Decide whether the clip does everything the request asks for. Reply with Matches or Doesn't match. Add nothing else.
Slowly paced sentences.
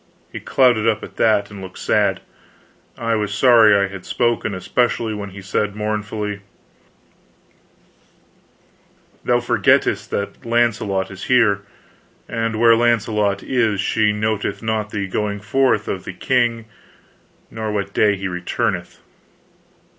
Matches